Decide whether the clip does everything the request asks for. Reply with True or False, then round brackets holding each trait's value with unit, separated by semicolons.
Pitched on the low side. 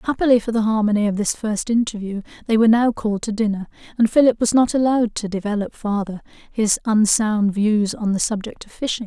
False (220 Hz)